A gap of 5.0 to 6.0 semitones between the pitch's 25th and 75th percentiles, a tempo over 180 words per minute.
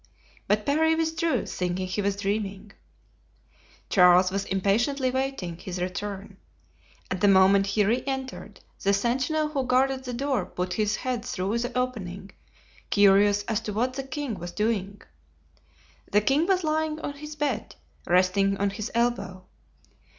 No: average, 5.3 semitones; average, 150 wpm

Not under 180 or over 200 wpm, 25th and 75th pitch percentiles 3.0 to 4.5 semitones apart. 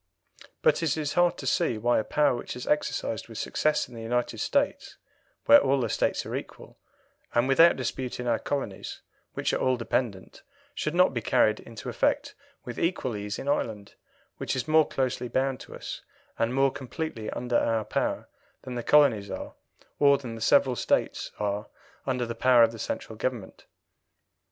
Yes: average, 185 wpm; average, 3.6 semitones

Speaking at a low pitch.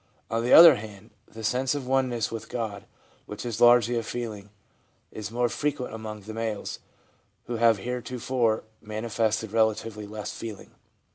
Yes: low, 115 Hz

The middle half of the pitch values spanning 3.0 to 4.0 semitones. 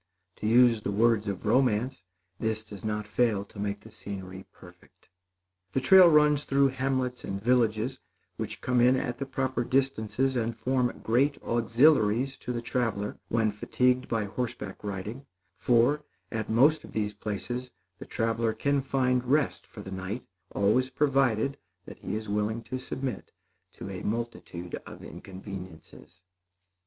Yes: average, 3.7 semitones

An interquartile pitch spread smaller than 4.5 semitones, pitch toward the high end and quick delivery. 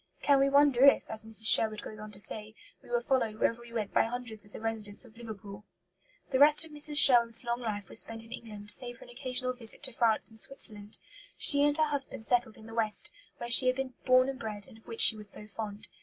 Yes: average, 2.9 semitones; high, 230 Hz; fast, 245 wpm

